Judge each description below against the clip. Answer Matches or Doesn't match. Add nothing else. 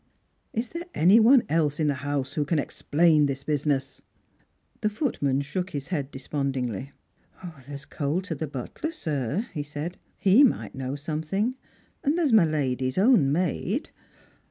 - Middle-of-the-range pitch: Matches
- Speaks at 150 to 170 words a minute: Matches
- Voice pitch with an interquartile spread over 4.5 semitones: Matches